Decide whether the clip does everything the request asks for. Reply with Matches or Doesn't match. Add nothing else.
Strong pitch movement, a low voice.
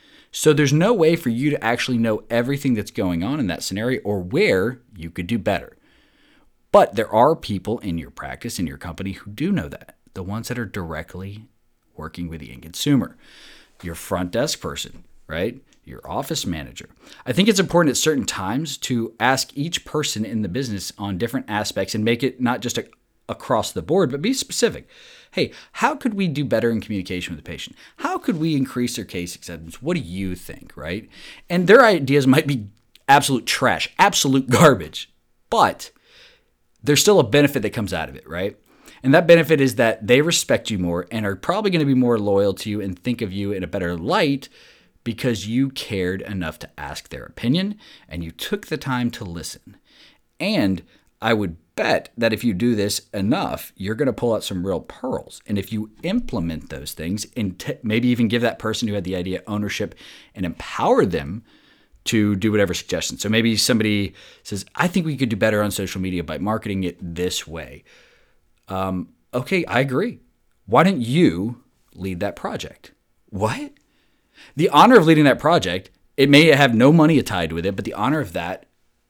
Matches